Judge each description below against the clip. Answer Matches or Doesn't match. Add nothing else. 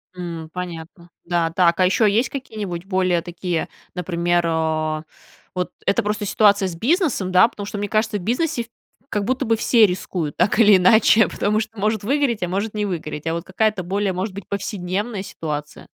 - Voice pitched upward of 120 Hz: Matches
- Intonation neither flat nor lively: Matches